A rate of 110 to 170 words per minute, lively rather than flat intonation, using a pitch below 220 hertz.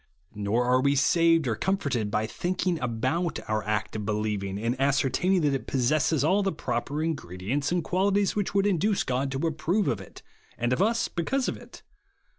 No: average, 195 wpm; wide, 7.3 semitones; medium, 140 Hz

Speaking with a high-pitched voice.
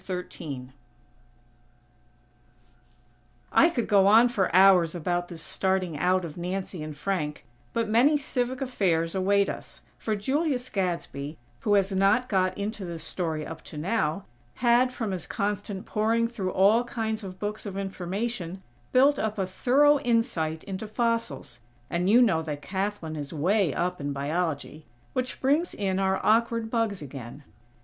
Yes: high, 195 Hz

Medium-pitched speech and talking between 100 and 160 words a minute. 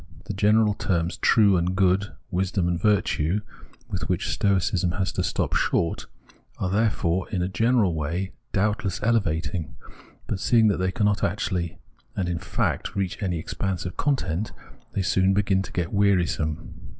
No: very low, 95 Hz; average, 155 wpm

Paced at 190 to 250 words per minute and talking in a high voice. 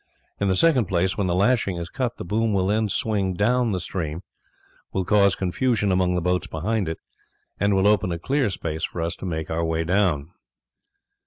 No: average, 200 wpm; very low, 95 Hz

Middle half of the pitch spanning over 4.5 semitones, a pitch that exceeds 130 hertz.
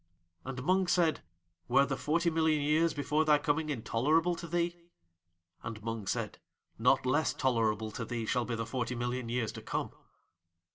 Yes: average, 5.2 semitones; medium, 140 Hz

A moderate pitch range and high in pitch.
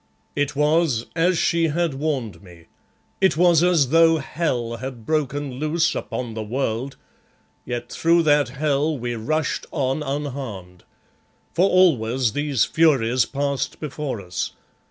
No: average, 4.6 semitones; medium, 140 Hz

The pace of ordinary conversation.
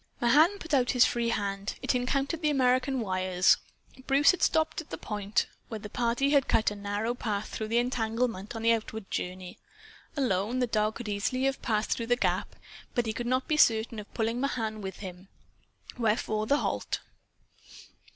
Yes: average, 185 wpm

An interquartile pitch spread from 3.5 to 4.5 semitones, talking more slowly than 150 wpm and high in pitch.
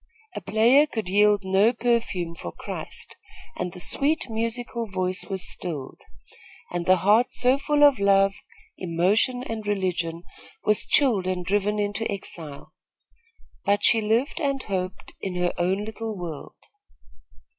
Yes: average, 3.9 semitones; average, 140 wpm; high, 205 Hz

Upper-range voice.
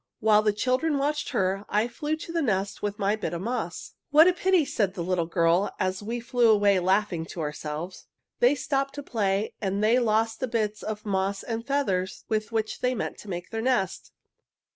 Yes: high, 215 Hz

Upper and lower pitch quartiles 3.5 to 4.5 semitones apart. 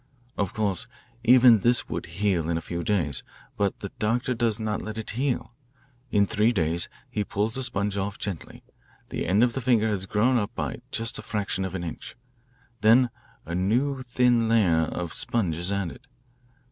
Yes: average, 3.9 semitones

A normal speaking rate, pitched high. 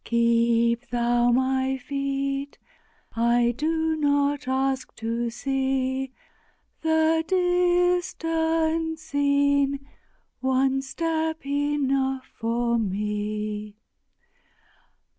No: slow, 70 wpm; very high, 270 Hz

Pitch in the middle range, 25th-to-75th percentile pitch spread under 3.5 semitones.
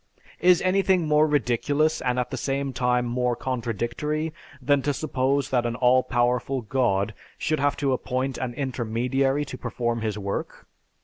No: low, 130 Hz; average, 2.9 semitones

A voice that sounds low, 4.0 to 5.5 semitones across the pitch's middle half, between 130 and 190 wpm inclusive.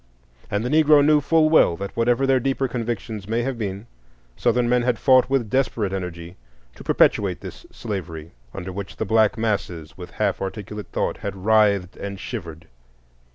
Yes: low, 110 Hz; average, 4.5 semitones; average, 170 wpm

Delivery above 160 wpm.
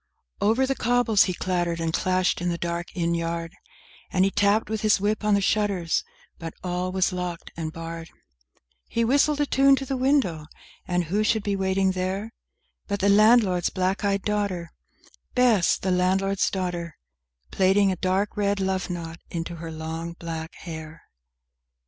Yes: average, 170 wpm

